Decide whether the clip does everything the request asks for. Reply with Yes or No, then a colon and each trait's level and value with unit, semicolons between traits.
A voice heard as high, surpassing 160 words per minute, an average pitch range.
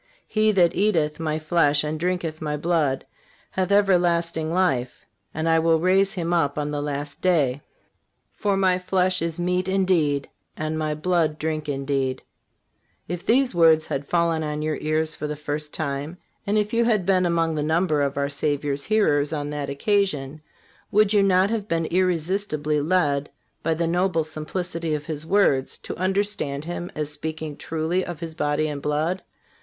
No: medium, 160 Hz; average, 170 wpm; average, 3.5 semitones